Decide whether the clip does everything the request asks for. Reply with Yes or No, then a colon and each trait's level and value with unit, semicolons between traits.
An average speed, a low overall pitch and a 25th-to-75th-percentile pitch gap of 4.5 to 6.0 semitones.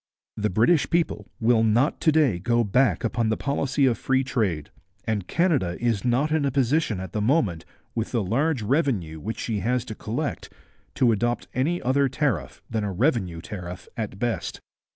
Yes: average, 180 wpm; low, 120 Hz; average, 4.8 semitones